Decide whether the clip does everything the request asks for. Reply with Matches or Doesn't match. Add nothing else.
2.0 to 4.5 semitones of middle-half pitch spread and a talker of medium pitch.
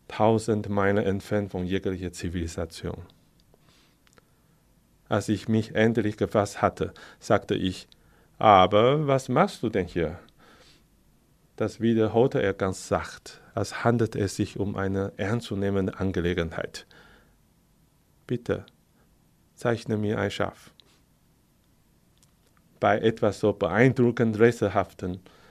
Doesn't match